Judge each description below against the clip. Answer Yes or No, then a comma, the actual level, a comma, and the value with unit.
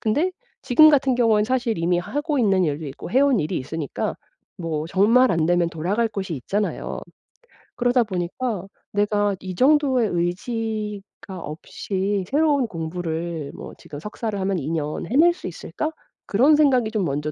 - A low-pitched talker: No, high, 205 Hz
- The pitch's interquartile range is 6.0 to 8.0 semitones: Yes, wide, 6.5 semitones